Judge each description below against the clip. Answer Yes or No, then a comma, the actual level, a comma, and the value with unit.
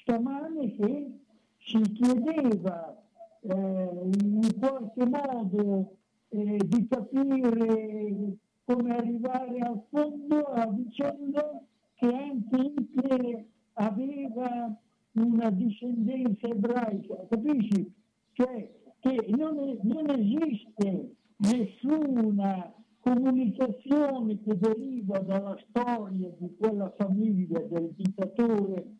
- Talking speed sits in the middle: No, slow, 85 wpm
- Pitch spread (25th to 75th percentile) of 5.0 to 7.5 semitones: No, average, 3.5 semitones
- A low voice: No, high, 230 Hz